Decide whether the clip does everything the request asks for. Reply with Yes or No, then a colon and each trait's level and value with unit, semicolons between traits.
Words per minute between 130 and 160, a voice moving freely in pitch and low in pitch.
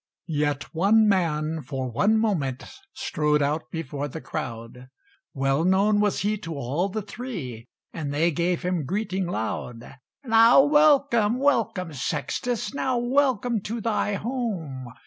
No: slow, 135 wpm; wide, 7.4 semitones; medium, 180 Hz